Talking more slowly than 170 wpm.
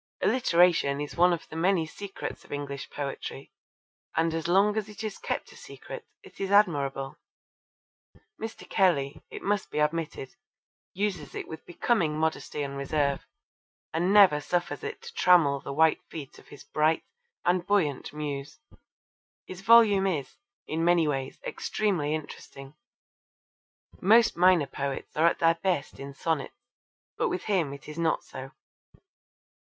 Yes: average, 150 wpm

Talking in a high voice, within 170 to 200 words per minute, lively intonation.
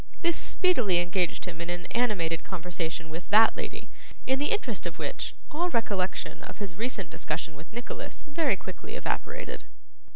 No: high, 195 Hz; average, 160 wpm; wide, 7.3 semitones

